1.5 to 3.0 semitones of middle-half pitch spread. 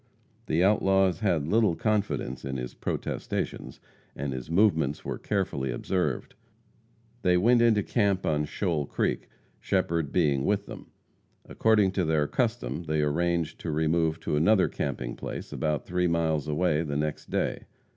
No: average, 4.5 semitones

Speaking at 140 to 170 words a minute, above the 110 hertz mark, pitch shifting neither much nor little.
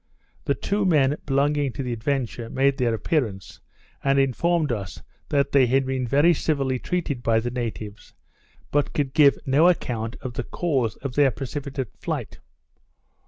Yes: average, 160 wpm; low, 135 Hz; average, 3.2 semitones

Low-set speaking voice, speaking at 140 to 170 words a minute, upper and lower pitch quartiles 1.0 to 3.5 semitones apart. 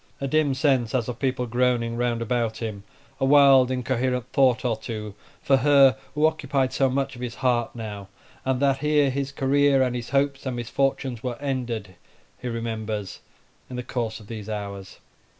No: low, 125 Hz; average, 180 wpm; average, 2.8 semitones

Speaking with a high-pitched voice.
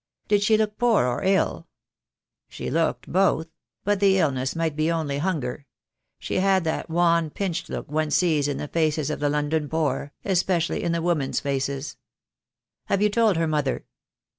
No: medium, 165 Hz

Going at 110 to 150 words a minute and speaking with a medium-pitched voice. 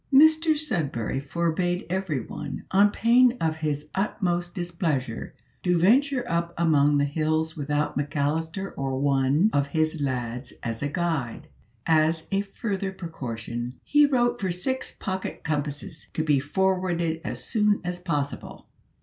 Yes: slow, 135 wpm; medium, 165 Hz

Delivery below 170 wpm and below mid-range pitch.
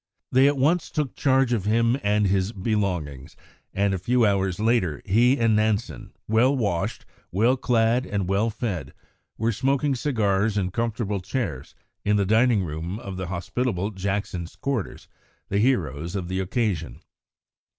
Yes: average, 150 wpm; low, 105 Hz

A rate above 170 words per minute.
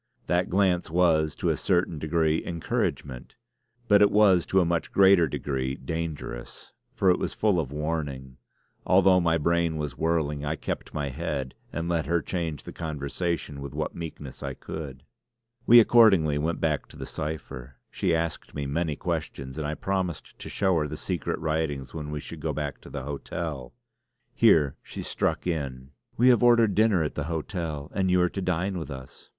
Yes: average, 185 wpm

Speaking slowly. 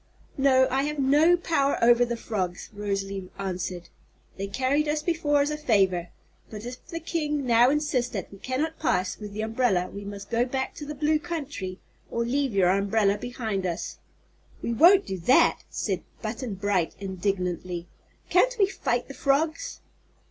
No: average, 170 wpm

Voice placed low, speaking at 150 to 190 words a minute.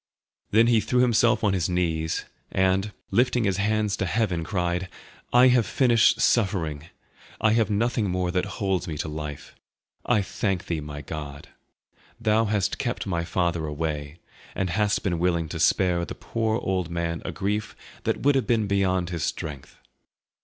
Yes: very low, 95 Hz; average, 165 wpm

